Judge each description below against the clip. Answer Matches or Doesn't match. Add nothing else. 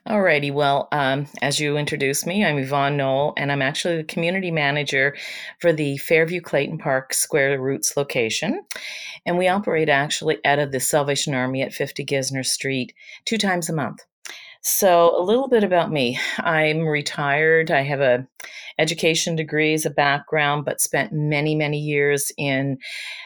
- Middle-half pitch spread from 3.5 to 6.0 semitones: Doesn't match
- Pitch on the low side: Doesn't match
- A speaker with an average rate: Matches